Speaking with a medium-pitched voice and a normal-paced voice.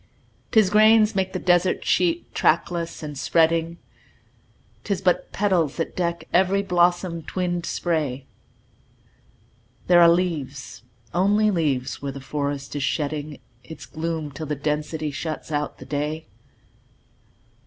No: medium, 165 Hz; slow, 125 wpm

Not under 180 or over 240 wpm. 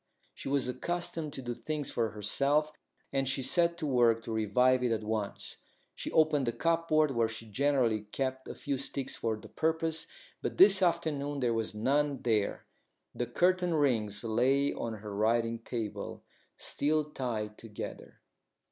No: average, 160 wpm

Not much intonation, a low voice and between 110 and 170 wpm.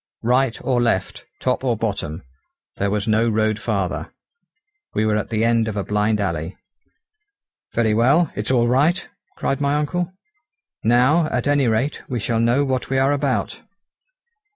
No: average, 3.8 semitones; low, 115 Hz; average, 160 wpm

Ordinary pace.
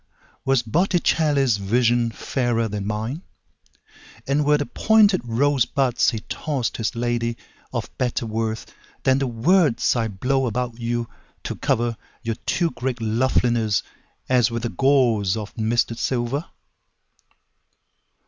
No: slow, 100 wpm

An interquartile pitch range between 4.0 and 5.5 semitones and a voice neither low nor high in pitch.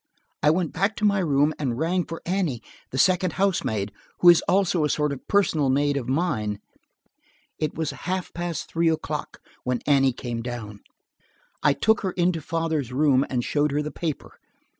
Yes: average, 4.7 semitones; medium, 150 Hz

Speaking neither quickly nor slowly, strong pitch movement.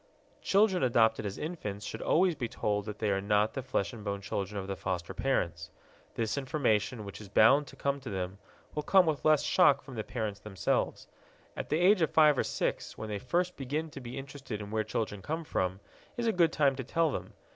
No: fast, 220 wpm; wide, 6.6 semitones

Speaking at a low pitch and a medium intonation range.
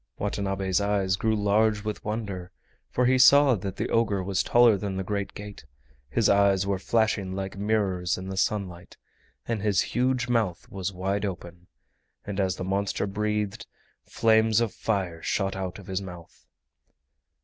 No: low, 100 Hz; narrow, 2.3 semitones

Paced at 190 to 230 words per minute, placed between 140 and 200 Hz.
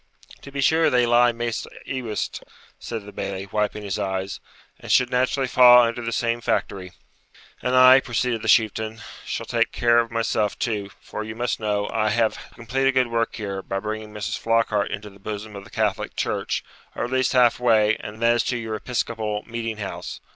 No: average, 195 wpm; low, 115 Hz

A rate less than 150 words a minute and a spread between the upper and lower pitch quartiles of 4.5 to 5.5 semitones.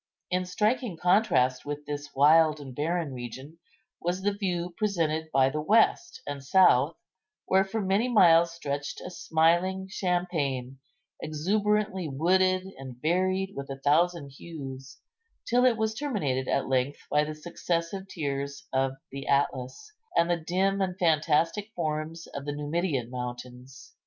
Yes: average, 140 wpm; average, 5.0 semitones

